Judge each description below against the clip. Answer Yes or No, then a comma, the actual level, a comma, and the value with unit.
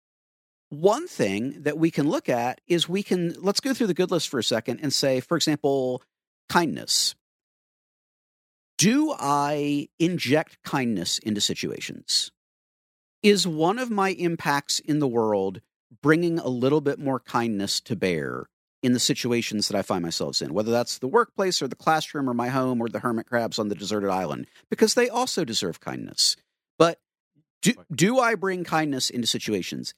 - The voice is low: No, medium, 145 Hz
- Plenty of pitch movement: Yes, wide, 6.3 semitones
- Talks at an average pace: Yes, average, 170 wpm